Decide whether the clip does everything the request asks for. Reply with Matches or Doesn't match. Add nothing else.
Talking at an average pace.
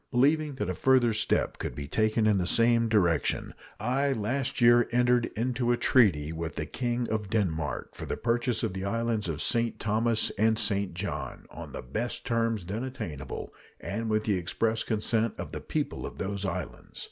Matches